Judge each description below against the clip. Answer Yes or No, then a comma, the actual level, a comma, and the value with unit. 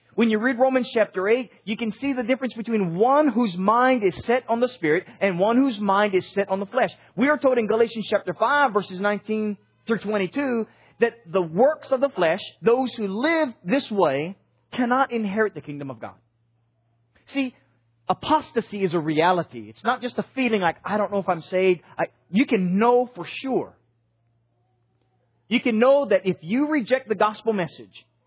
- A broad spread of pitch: Yes, wide, 6.2 semitones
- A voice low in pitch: No, high, 210 Hz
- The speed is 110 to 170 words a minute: No, average, 190 wpm